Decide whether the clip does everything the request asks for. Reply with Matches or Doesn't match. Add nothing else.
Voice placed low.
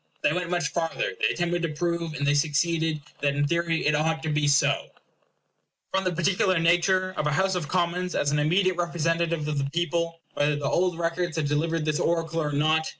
Doesn't match